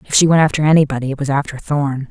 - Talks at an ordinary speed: No, fast, 255 wpm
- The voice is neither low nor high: Yes, medium, 145 Hz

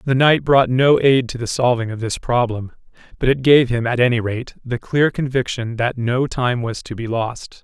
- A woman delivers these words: No, male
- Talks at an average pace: No, fast, 220 wpm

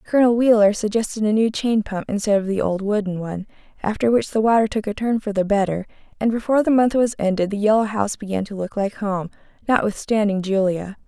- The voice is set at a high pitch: Yes, high, 210 Hz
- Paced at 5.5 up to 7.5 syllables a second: Yes, 6.1 syllables/s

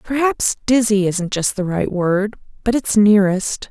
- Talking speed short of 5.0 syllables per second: Yes, 4.3 syllables/s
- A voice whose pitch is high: Yes, high, 210 Hz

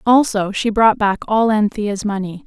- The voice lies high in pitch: Yes, high, 210 Hz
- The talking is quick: No, average, 170 wpm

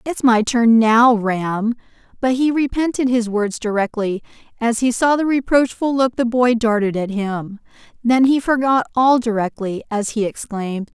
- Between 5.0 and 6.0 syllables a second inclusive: No, 4.5 syllables/s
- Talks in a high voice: Yes, high, 235 Hz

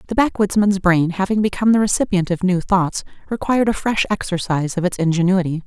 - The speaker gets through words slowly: No, average, 180 wpm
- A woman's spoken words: Yes, female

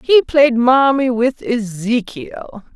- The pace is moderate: No, slow, 110 wpm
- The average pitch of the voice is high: Yes, high, 245 Hz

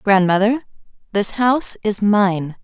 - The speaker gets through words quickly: No, slow, 115 wpm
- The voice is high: Yes, high, 205 Hz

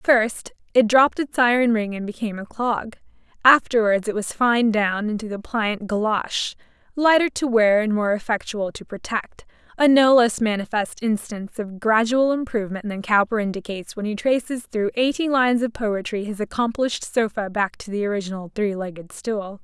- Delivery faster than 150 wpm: Yes, average, 165 wpm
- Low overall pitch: No, high, 220 Hz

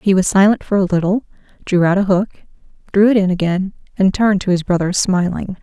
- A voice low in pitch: No, high, 190 Hz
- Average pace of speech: No, fast, 215 wpm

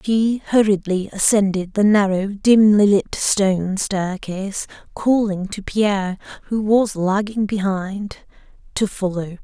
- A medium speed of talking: No, slow, 115 wpm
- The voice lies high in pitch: Yes, high, 200 Hz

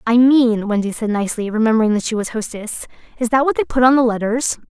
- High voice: Yes, high, 230 Hz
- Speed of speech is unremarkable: No, fast, 230 wpm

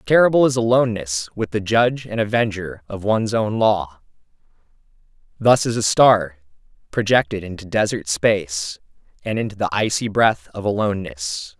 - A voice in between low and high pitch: No, low, 105 Hz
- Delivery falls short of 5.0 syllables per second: No, 5.1 syllables/s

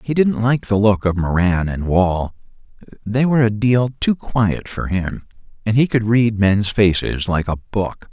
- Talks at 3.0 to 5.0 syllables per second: Yes, 4.2 syllables/s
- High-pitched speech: No, low, 105 Hz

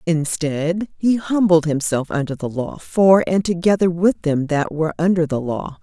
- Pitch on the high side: No, medium, 165 Hz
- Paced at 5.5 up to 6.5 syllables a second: No, 4.5 syllables/s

